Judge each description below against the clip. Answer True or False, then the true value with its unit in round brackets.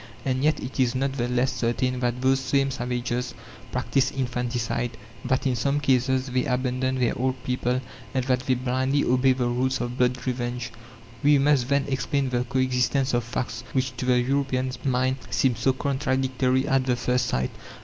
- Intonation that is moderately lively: False (1.2 semitones)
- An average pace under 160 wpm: False (180 wpm)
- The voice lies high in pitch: False (130 Hz)